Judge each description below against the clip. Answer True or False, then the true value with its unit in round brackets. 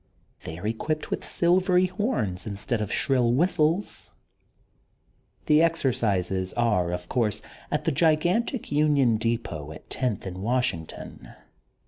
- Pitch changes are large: True (8.3 semitones)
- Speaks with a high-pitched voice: False (125 Hz)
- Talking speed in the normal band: False (120 wpm)